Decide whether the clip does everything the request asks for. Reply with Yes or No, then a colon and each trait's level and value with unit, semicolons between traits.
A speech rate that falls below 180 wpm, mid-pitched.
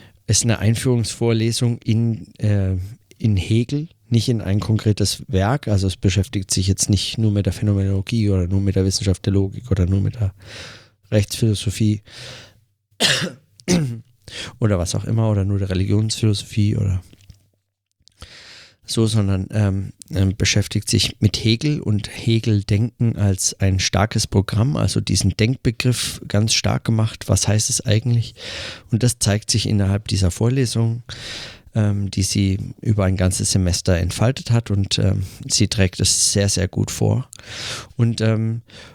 No: average, 145 wpm; low, 105 Hz